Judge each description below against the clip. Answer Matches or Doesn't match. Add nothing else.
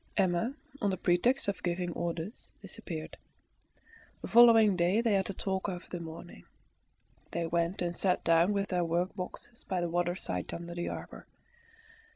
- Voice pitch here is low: Doesn't match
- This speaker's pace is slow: Doesn't match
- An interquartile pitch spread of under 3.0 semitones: Matches